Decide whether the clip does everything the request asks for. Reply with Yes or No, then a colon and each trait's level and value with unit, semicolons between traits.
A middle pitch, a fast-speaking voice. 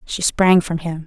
Yes: medium, 170 Hz; fast, 225 wpm